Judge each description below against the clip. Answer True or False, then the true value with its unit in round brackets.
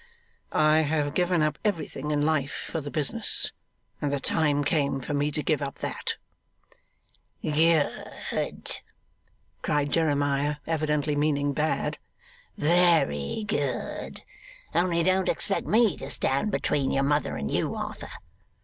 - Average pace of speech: False (130 wpm)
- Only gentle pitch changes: True (2.3 semitones)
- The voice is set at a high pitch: False (150 Hz)